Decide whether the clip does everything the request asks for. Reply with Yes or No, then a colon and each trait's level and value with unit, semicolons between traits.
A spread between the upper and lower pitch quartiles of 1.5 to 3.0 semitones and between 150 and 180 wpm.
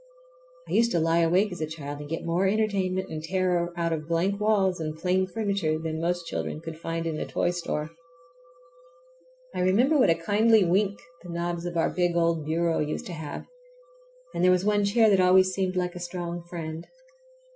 No: narrow, 2.4 semitones; average, 200 wpm